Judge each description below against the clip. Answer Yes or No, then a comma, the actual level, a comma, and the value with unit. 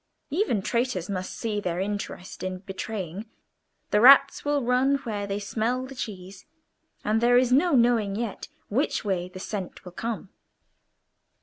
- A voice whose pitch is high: Yes, high, 215 Hz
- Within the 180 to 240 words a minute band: No, average, 150 wpm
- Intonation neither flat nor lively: Yes, average, 4.4 semitones